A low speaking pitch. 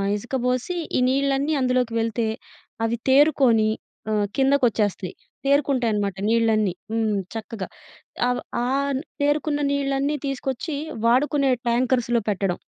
No: very high, 250 Hz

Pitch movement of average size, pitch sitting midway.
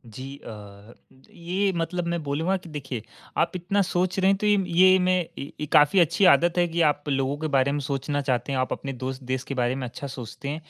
Yes: average, 5.0 semitones; medium, 145 Hz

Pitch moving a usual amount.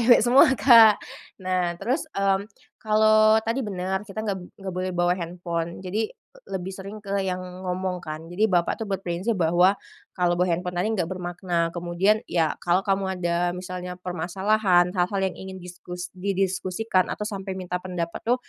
No: narrow, 2.1 semitones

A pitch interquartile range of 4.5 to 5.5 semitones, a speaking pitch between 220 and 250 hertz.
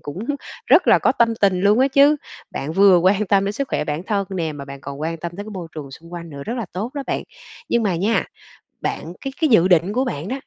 No: average, 5.0 semitones; high, 190 Hz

